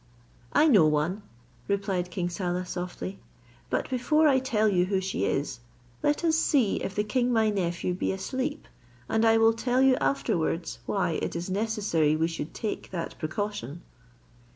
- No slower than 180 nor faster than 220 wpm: No, average, 165 wpm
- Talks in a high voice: Yes, high, 195 Hz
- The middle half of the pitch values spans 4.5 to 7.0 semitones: Yes, average, 4.9 semitones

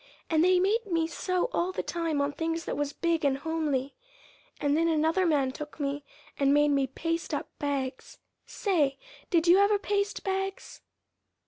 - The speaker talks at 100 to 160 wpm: No, average, 175 wpm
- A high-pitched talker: Yes, very high, 325 Hz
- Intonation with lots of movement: No, average, 4.0 semitones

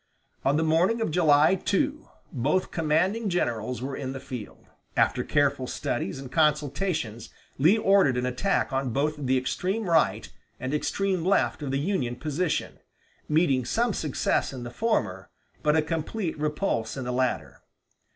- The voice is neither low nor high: Yes, medium, 150 Hz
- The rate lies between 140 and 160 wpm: Yes, average, 155 wpm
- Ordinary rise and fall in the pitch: No, wide, 5.8 semitones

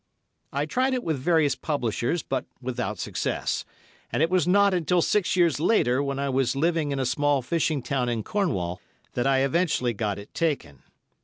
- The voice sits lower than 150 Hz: Yes, medium, 140 Hz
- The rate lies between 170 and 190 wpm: Yes, average, 180 wpm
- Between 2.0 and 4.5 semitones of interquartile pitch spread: No, average, 5.1 semitones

